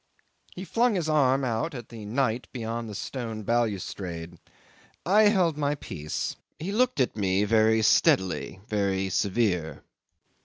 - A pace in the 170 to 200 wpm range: No, average, 140 wpm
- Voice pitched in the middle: No, low, 115 Hz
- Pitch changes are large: Yes, wide, 6.4 semitones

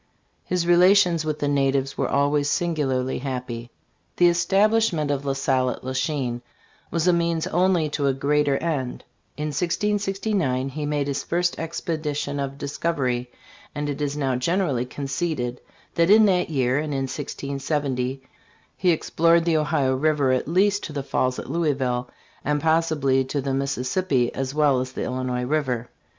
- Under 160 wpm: No, average, 165 wpm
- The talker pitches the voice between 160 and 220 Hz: No, medium, 145 Hz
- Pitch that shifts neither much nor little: Yes, average, 4.0 semitones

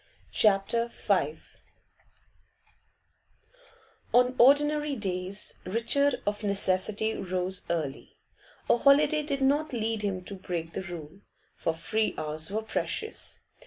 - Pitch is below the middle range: No, high, 210 Hz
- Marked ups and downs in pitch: Yes, wide, 6.2 semitones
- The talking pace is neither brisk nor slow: No, slow, 110 wpm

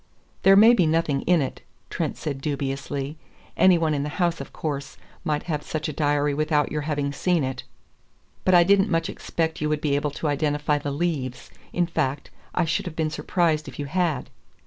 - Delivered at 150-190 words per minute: No, average, 200 wpm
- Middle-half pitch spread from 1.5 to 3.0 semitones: Yes, narrow, 2.5 semitones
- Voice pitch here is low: No, medium, 150 Hz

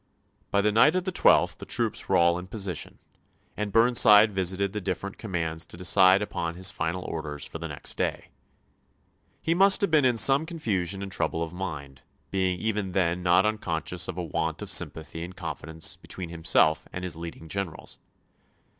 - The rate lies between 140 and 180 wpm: No, average, 200 wpm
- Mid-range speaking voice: No, very low, 90 Hz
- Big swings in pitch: No, average, 3.9 semitones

